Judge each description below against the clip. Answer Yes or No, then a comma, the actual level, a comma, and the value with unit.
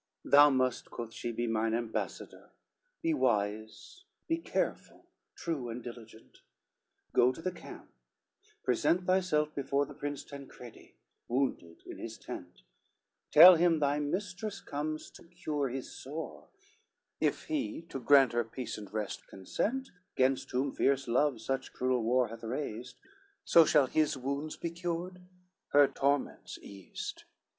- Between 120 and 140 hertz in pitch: Yes, low, 135 Hz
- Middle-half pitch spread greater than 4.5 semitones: Yes, average, 4.9 semitones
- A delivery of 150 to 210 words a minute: No, average, 140 wpm